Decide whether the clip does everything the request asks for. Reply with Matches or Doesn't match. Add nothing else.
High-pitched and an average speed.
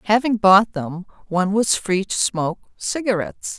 Matches